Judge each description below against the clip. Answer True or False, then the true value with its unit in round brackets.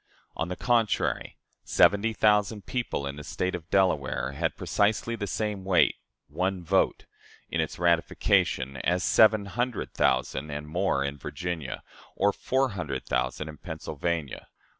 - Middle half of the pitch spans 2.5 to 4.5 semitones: False (5.4 semitones)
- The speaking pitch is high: False (90 Hz)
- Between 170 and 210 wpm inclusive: False (140 wpm)